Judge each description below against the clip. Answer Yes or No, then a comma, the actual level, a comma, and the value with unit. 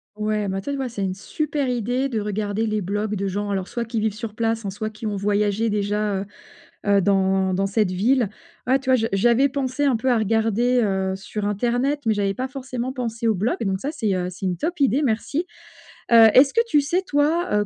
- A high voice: Yes, high, 220 Hz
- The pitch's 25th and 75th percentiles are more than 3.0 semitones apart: Yes, average, 4.0 semitones